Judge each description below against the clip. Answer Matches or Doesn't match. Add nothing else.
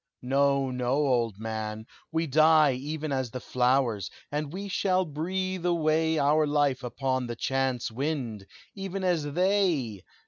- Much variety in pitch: Doesn't match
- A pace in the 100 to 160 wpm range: Matches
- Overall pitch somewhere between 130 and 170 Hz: Matches